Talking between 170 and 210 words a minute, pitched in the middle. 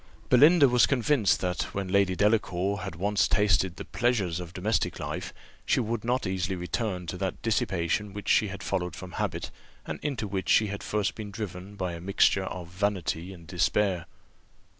No: average, 180 wpm; very low, 95 Hz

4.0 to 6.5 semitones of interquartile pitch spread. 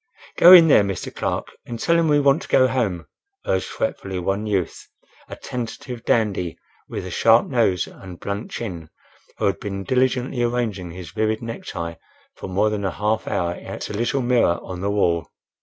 Yes: average, 4.7 semitones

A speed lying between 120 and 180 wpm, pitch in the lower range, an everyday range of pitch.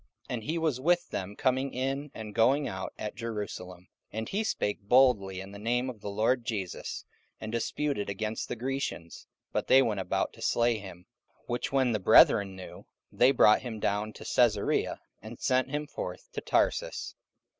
No: average, 190 wpm; low, 115 Hz; average, 4.4 semitones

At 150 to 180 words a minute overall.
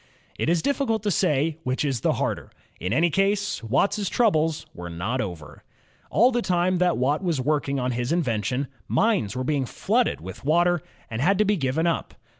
No: average, 190 wpm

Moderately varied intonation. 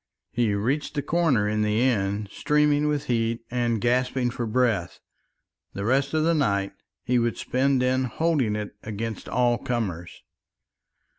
Yes: average, 4.2 semitones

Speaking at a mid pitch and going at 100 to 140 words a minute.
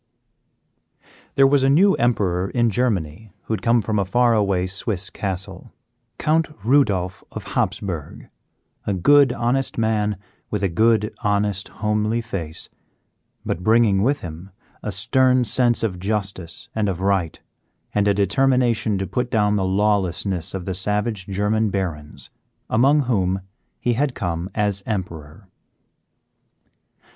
No: low, 105 Hz; slow, 135 wpm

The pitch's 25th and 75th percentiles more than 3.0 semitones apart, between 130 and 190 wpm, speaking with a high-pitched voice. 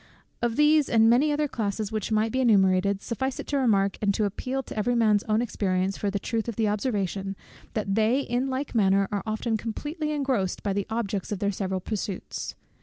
No: average, 3.6 semitones; fast, 205 wpm; high, 215 Hz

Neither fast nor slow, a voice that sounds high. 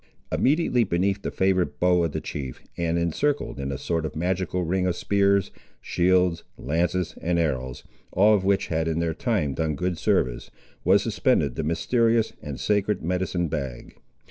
No: average, 170 wpm; very low, 90 Hz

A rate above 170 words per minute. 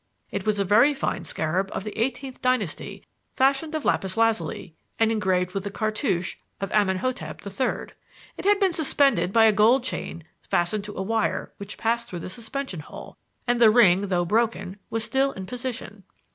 Yes: average, 180 wpm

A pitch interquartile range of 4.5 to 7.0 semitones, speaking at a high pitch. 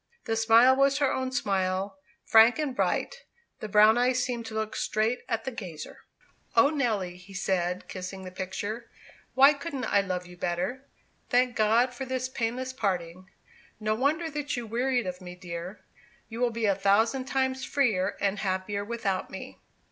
Yes: average, 5.2 semitones; high, 225 Hz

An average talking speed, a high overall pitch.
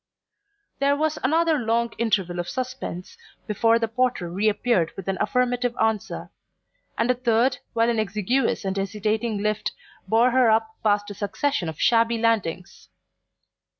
Yes: average, 145 wpm; high, 225 Hz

